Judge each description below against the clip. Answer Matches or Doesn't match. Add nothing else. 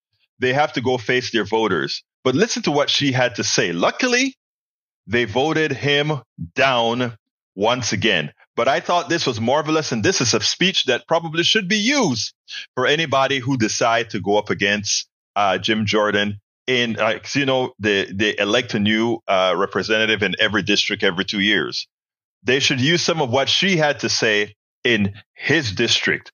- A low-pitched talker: Matches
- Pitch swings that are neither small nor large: Doesn't match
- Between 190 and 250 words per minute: Doesn't match